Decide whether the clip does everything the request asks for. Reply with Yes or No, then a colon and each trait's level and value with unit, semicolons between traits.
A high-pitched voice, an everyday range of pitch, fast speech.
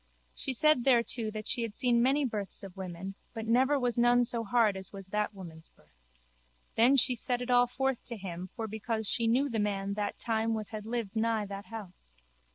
Yes: high, 225 Hz; average, 3.5 semitones; fast, 210 wpm